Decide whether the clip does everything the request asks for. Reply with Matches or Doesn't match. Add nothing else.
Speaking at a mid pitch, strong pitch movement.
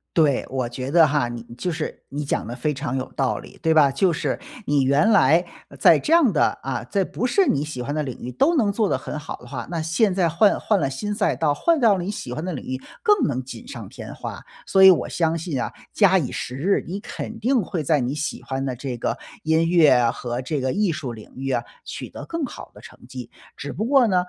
Matches